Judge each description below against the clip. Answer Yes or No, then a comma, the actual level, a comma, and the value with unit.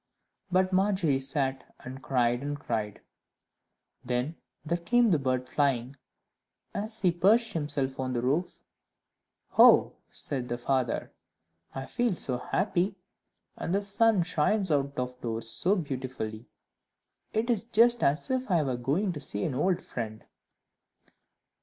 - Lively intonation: Yes, wide, 7.0 semitones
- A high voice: No, medium, 145 Hz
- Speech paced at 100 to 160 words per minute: Yes, average, 140 wpm